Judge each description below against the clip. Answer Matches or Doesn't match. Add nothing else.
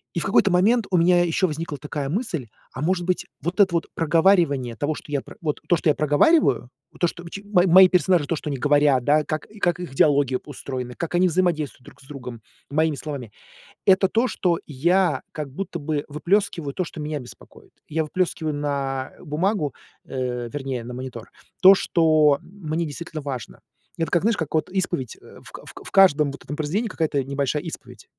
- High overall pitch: Doesn't match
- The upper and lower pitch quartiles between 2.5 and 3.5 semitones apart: Doesn't match